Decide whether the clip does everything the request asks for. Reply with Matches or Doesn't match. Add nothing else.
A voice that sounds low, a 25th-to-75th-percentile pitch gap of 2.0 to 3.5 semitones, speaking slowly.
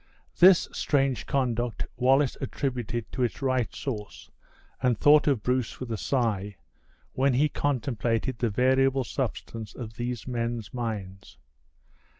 Matches